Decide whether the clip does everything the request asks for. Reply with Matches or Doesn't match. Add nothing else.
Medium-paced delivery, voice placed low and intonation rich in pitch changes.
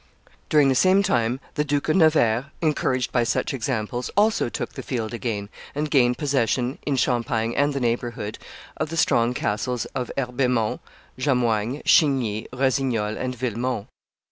Doesn't match